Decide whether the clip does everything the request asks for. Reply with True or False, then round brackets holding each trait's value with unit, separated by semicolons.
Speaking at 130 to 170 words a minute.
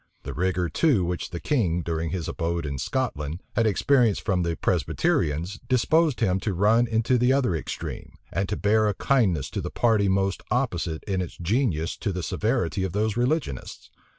False (180 wpm)